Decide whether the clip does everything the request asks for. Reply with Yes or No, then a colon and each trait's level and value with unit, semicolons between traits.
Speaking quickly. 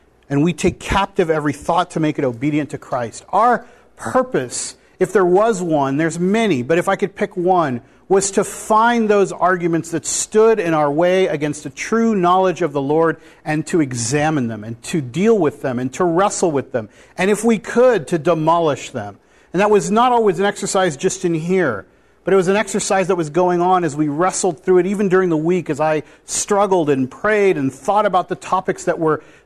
Yes: fast, 210 wpm